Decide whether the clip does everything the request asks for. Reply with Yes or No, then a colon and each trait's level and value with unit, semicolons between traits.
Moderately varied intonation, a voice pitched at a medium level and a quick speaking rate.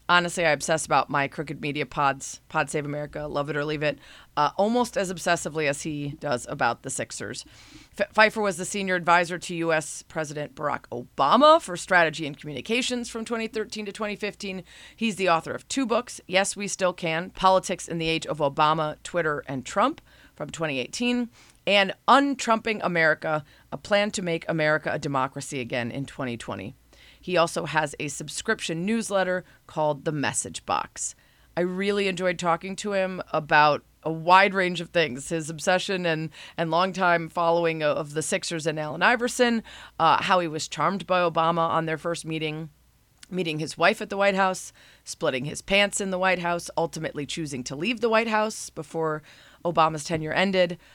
No: average, 3.9 semitones; medium, 170 Hz; average, 175 wpm